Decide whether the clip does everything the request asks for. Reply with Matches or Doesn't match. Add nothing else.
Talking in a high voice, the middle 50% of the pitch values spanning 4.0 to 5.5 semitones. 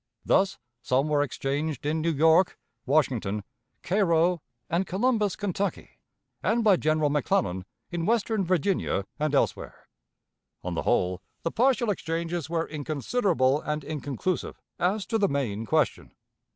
Doesn't match